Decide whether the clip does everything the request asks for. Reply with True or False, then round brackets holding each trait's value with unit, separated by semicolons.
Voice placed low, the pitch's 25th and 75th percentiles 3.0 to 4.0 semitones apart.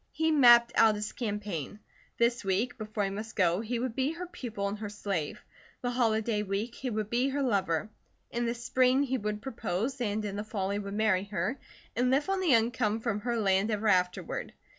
False (220 Hz; 3.3 semitones)